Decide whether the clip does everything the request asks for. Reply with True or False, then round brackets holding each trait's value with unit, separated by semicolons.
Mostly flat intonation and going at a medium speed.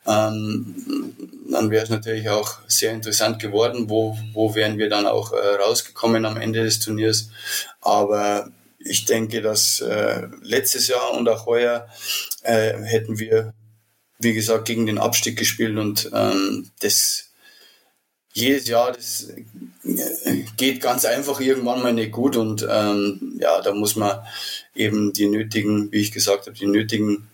True (1.6 semitones; 150 wpm)